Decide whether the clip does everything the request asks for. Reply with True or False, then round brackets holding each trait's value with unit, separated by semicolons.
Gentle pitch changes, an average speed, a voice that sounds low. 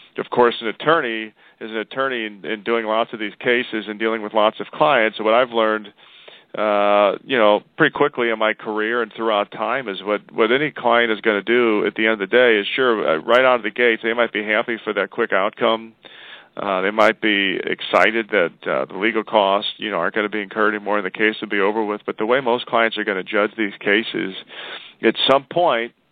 False (1.7 semitones; 240 wpm; 110 Hz)